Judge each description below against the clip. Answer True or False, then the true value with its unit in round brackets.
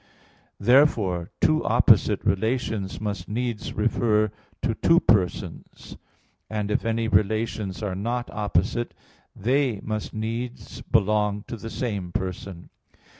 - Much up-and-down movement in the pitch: False (2.8 semitones)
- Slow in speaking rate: True (115 wpm)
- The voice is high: False (110 Hz)